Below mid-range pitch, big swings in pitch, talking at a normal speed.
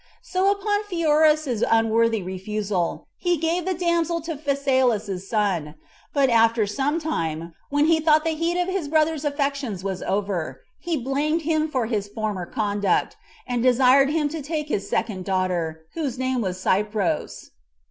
No: very high, 260 Hz; wide, 7.5 semitones; average, 155 wpm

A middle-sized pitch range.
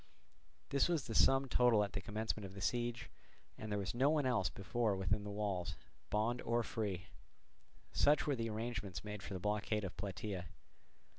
Yes: average, 3.3 semitones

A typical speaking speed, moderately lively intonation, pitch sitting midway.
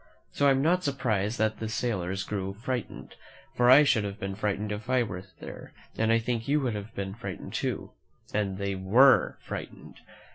No: average, 195 wpm; average, 4.0 semitones; low, 110 Hz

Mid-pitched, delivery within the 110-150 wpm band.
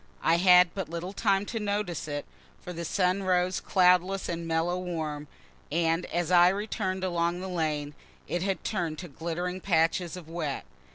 No: medium, 175 Hz; average, 170 wpm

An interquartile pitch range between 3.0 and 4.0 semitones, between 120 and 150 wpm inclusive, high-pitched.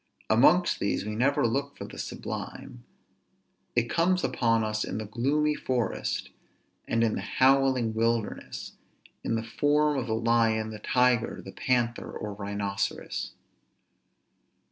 No: average, 3.3 semitones; slow, 135 wpm; low, 115 Hz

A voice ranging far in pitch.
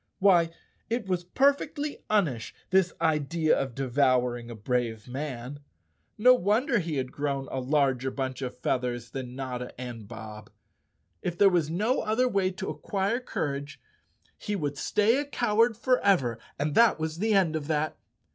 Yes: wide, 7.8 semitones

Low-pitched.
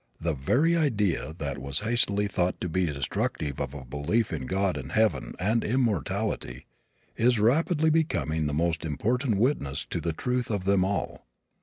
Yes: very low, 95 Hz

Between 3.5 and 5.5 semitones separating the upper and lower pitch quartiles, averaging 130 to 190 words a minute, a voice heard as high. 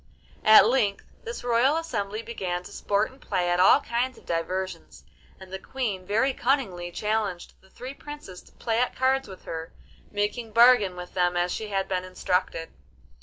Yes: average, 5.1 semitones; average, 175 wpm; high, 205 Hz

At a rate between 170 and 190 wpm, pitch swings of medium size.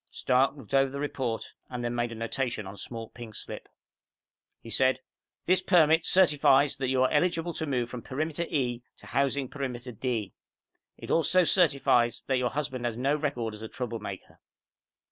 Yes: average, 180 wpm; average, 3.6 semitones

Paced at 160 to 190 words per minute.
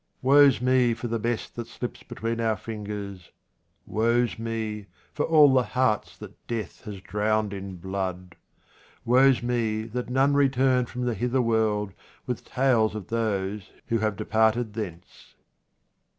No: average, 145 wpm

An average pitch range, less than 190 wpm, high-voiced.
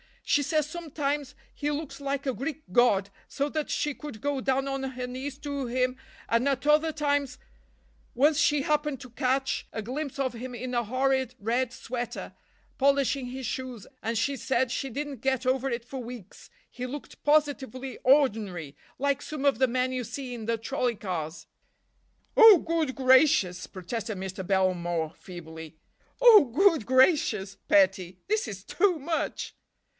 Yes: average, 4.1 semitones; average, 160 wpm; very high, 260 Hz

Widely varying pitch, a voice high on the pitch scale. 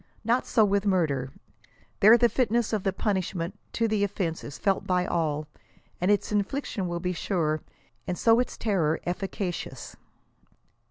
No: average, 3.7 semitones; high, 195 Hz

